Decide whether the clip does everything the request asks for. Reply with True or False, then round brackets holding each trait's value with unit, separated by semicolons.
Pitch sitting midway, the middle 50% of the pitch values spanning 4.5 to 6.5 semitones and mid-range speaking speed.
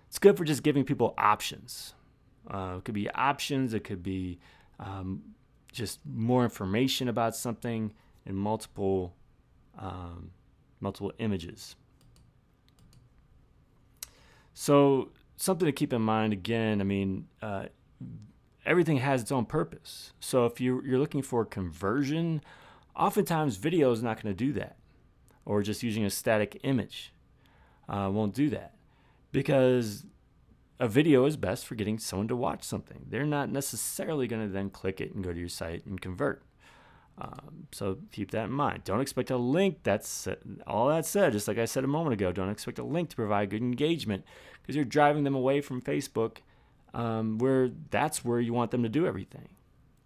False (115 Hz; 5.0 semitones; 165 wpm)